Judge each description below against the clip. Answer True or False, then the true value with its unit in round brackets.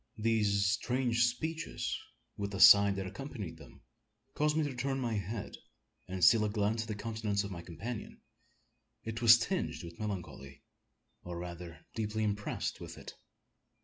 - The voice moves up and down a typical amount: True (3.1 semitones)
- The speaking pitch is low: True (105 Hz)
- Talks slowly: False (155 wpm)